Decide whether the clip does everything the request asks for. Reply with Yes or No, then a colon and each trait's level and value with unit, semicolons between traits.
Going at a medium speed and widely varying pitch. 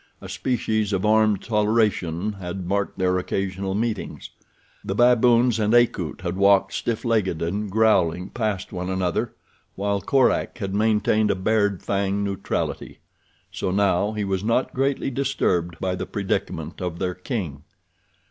No: average, 145 wpm; average, 2.8 semitones